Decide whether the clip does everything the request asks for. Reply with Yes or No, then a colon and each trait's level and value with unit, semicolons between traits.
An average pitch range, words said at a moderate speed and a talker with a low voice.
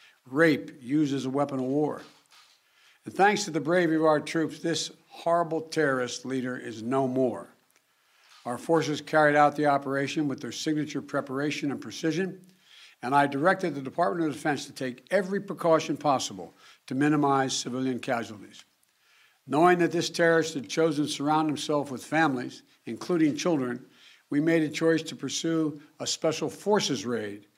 No: average, 3.0 semitones; average, 160 wpm; medium, 150 Hz